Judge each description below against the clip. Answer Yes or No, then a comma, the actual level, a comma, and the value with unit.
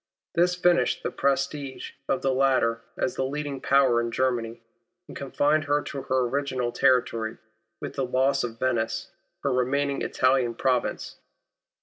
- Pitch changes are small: Yes, narrow, 2.2 semitones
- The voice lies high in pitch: No, low, 130 Hz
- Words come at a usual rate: Yes, average, 145 wpm